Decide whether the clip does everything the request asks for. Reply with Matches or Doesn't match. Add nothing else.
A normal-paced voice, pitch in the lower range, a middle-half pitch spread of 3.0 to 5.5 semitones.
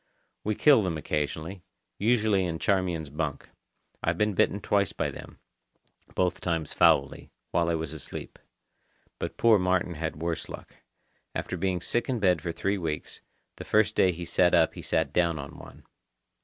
Matches